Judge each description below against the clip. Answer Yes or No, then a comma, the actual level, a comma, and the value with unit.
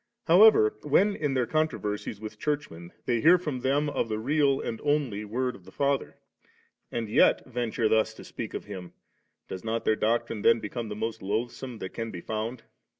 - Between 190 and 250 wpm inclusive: Yes, average, 195 wpm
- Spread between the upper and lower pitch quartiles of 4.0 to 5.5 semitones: Yes, average, 4.6 semitones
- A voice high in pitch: No, low, 115 Hz